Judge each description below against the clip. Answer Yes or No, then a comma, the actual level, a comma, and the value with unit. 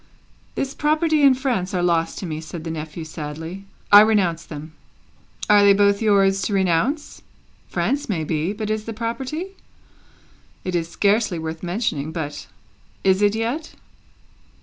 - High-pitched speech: Yes, high, 195 Hz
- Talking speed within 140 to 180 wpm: Yes, average, 150 wpm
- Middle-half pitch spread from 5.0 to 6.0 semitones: Yes, wide, 5.5 semitones